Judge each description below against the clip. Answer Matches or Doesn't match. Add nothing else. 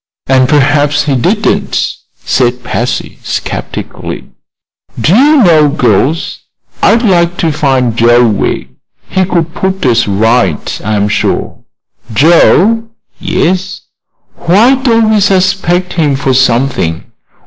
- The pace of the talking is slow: Matches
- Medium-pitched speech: Matches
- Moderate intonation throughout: Doesn't match